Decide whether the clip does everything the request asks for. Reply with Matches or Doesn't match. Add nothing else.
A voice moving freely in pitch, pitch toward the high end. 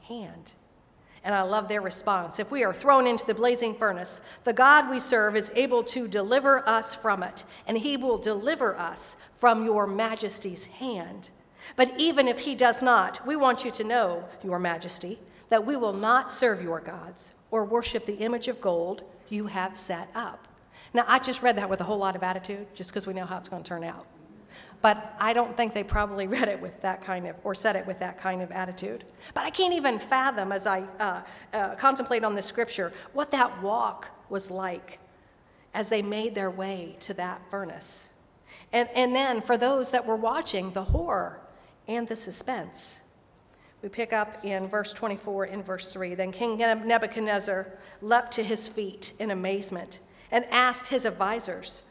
Doesn't match